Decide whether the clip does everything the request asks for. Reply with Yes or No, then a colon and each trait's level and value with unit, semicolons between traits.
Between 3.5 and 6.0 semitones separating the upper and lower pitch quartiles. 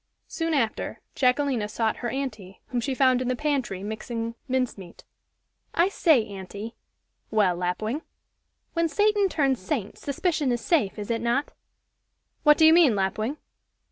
Yes: wide, 5.4 semitones